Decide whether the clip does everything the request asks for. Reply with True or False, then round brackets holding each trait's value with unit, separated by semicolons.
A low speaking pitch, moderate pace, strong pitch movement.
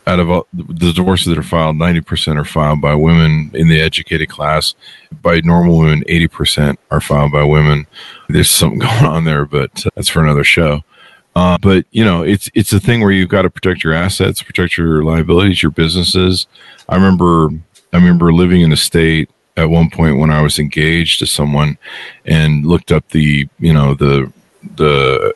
False (80 Hz; 195 wpm; 2.8 semitones)